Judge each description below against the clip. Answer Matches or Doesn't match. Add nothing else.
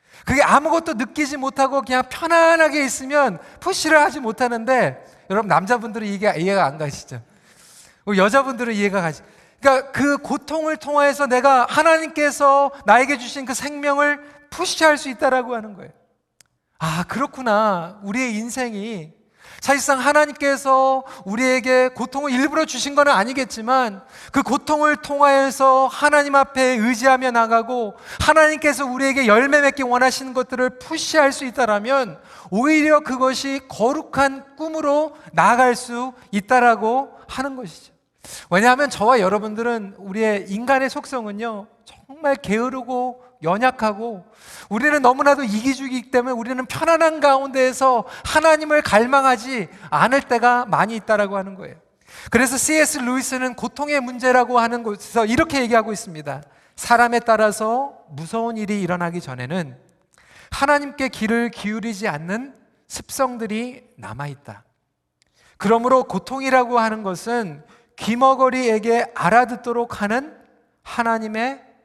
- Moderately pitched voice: Doesn't match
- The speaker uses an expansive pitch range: Doesn't match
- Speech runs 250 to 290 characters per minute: Doesn't match